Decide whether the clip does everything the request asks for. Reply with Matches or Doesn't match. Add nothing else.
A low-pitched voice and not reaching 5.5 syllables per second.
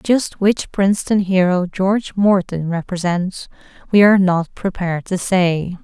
Doesn't match